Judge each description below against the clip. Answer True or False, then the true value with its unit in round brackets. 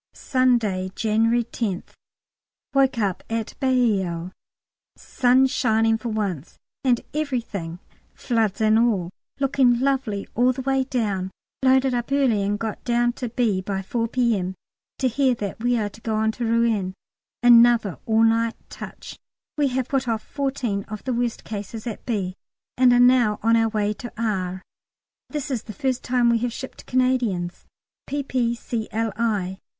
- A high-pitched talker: True (230 Hz)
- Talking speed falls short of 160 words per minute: True (150 wpm)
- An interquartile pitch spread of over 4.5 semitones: False (3.2 semitones)